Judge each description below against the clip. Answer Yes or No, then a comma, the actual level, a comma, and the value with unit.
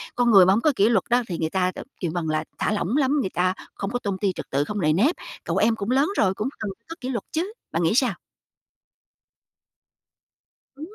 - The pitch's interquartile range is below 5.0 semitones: No, average, 5.3 semitones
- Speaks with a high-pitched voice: Yes, high, 205 Hz